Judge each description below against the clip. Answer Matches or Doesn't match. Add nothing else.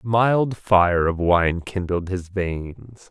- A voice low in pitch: Matches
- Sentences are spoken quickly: Doesn't match